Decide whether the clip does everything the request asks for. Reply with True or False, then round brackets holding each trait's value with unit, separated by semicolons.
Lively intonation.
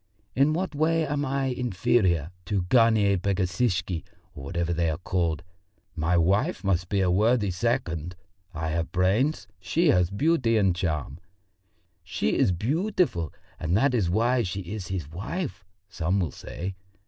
True (6.3 semitones)